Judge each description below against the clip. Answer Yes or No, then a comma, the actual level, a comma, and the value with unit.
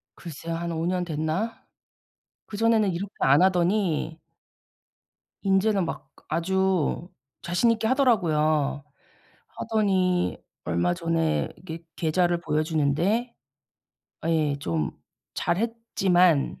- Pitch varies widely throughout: No, average, 3.7 semitones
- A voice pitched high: No, medium, 175 Hz